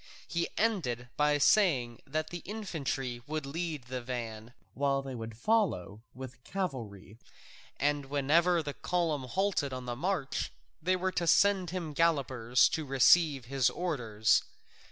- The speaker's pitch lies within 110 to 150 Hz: Yes, medium, 140 Hz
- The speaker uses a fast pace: No, average, 145 wpm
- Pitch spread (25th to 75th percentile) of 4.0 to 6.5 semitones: Yes, wide, 5.6 semitones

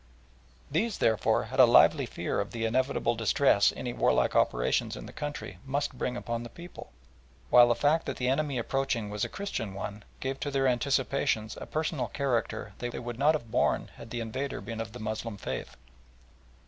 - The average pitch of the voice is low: Yes, low, 120 Hz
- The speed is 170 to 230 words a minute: Yes, average, 185 wpm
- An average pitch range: Yes, average, 3.6 semitones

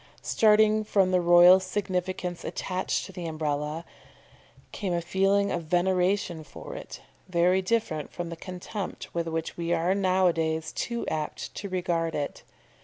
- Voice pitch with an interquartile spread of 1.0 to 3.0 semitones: Yes, narrow, 2.4 semitones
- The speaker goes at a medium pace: Yes, average, 155 wpm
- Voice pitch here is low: No, medium, 180 Hz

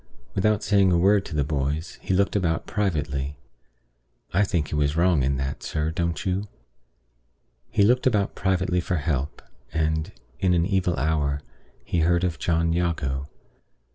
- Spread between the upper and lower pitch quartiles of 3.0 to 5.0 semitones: Yes, average, 4.2 semitones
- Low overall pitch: Yes, very low, 85 Hz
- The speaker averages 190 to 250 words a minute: No, average, 160 wpm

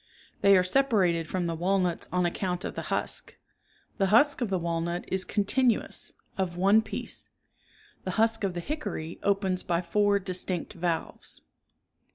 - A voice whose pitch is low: No, medium, 185 Hz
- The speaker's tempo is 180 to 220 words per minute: No, average, 160 wpm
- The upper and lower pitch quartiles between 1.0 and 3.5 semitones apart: Yes, average, 2.7 semitones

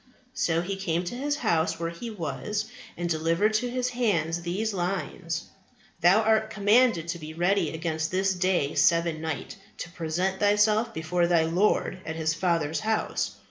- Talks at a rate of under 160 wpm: No, average, 165 wpm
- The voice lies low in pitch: No, medium, 175 Hz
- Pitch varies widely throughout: No, average, 4.2 semitones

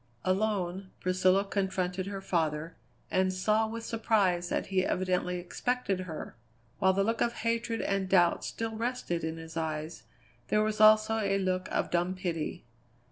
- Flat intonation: No, average, 3.3 semitones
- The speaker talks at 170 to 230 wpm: No, average, 155 wpm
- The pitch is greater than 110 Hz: Yes, high, 190 Hz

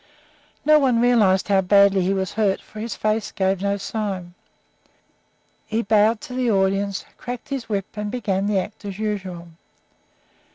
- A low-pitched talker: No, high, 205 Hz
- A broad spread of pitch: No, narrow, 2.4 semitones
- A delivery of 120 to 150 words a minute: No, average, 160 wpm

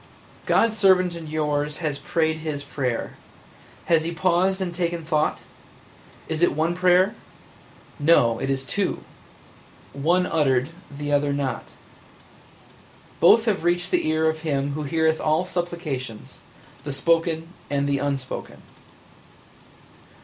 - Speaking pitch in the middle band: Yes, medium, 160 Hz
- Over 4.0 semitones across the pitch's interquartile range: No, average, 3.4 semitones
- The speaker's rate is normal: No, slow, 130 wpm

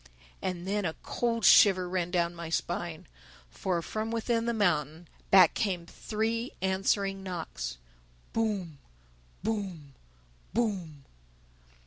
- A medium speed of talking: No, slow, 110 wpm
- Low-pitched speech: No, medium, 185 Hz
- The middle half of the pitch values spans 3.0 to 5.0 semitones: Yes, average, 4.1 semitones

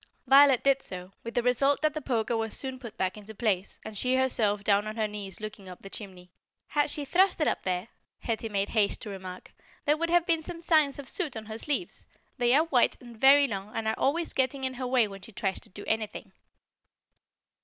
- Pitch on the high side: Yes, high, 235 Hz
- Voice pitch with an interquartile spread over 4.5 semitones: Yes, average, 5.1 semitones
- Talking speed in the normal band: No, fast, 230 wpm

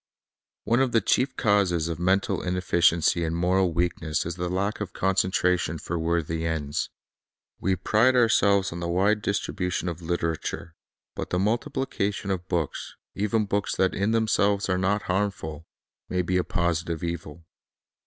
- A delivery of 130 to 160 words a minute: Yes, average, 155 wpm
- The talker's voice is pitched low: Yes, very low, 90 Hz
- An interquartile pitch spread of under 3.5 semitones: Yes, average, 3.1 semitones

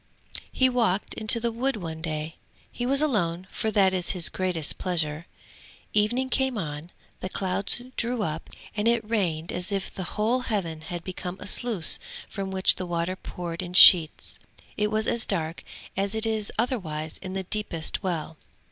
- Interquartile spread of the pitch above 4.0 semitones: Yes, average, 4.6 semitones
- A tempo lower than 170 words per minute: No, average, 175 wpm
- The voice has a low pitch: No, high, 190 Hz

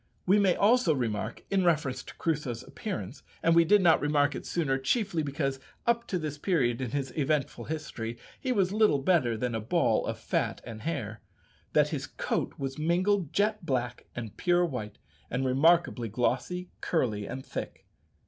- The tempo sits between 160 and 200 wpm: Yes, average, 175 wpm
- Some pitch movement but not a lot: No, wide, 6.1 semitones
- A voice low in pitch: No, medium, 145 Hz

